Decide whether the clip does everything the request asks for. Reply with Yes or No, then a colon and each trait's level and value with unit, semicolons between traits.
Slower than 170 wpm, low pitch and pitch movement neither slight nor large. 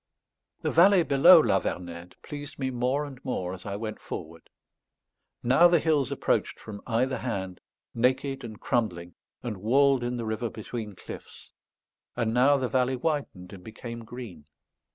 Yes: average, 155 wpm; low, 120 Hz; average, 4.6 semitones